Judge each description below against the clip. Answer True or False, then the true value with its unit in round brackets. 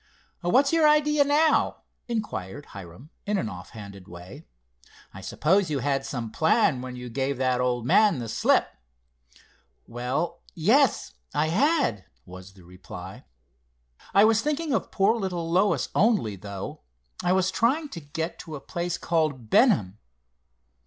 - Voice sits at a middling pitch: True (155 Hz)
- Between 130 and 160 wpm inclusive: True (145 wpm)